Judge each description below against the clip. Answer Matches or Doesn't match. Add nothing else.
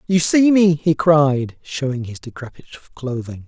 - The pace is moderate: Matches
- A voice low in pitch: Doesn't match